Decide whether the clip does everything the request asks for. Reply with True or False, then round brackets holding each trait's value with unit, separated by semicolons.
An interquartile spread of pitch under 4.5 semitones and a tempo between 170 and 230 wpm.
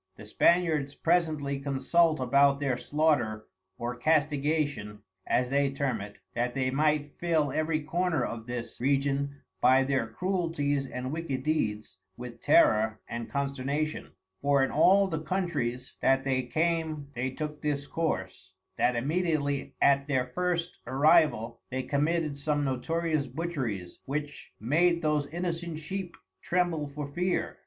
False (3.7 semitones; 135 wpm)